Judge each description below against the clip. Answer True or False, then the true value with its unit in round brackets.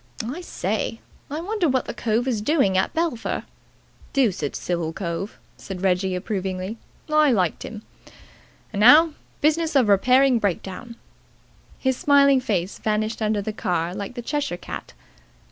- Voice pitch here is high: True (220 Hz)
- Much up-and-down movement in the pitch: True (6.3 semitones)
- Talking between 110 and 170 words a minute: True (145 wpm)